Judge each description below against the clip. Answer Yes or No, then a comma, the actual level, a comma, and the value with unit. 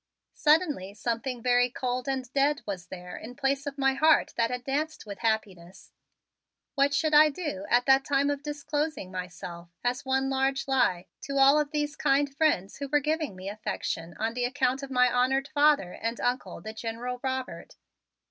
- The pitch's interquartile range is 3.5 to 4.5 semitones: Yes, average, 4.0 semitones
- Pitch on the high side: Yes, very high, 265 Hz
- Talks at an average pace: Yes, average, 180 wpm